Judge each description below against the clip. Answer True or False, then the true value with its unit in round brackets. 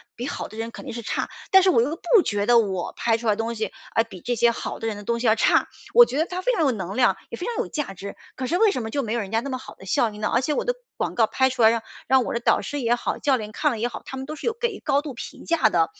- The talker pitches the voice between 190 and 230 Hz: False (240 Hz)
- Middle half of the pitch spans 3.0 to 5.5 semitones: True (4.6 semitones)